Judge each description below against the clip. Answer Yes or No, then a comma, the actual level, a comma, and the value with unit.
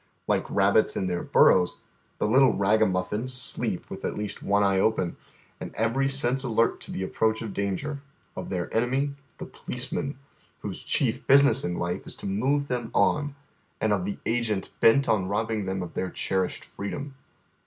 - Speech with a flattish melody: No, average, 5.1 semitones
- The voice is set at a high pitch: No, low, 110 Hz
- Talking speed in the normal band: Yes, average, 175 wpm